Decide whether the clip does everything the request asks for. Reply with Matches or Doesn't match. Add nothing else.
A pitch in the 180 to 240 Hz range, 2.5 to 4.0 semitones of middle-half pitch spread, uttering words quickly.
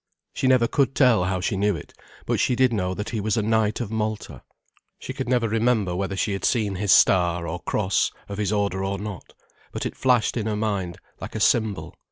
Doesn't match